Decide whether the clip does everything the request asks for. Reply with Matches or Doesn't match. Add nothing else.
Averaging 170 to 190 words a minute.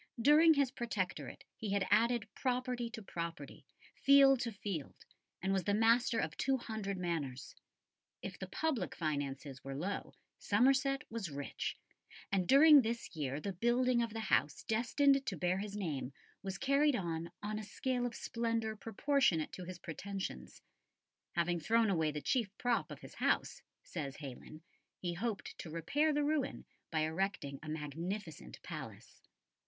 Doesn't match